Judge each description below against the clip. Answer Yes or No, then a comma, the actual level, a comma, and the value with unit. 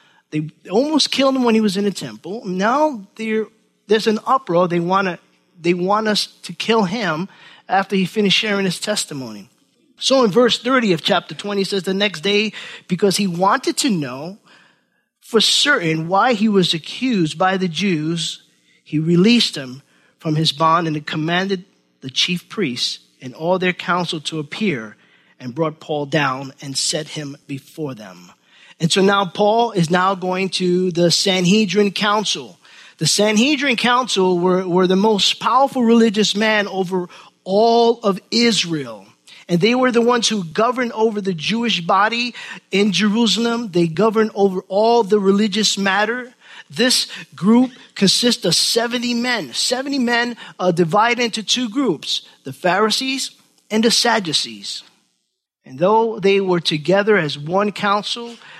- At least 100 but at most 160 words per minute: Yes, average, 155 wpm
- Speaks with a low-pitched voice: No, high, 200 Hz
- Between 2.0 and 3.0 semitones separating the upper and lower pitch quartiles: No, average, 4.4 semitones